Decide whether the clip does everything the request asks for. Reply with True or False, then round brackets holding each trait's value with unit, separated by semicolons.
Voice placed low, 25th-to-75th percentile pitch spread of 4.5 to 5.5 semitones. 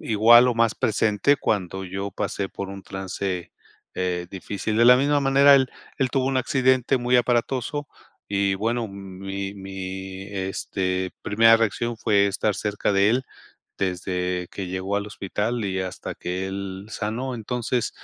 False (100 Hz; 3.8 semitones)